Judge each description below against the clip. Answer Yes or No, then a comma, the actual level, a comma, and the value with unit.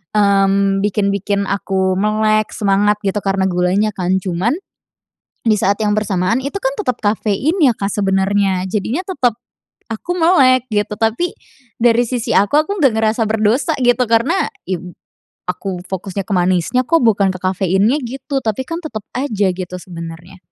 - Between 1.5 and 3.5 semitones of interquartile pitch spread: No, average, 4.1 semitones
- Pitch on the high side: Yes, high, 210 Hz